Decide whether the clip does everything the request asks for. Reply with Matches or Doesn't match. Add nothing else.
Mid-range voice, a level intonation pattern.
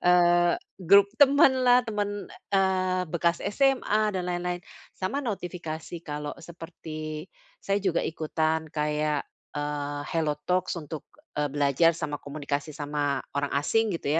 Doesn't match